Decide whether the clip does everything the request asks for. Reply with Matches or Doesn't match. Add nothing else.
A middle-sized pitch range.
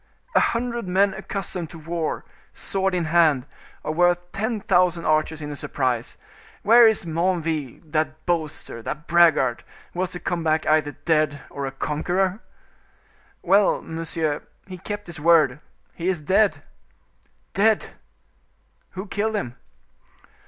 Matches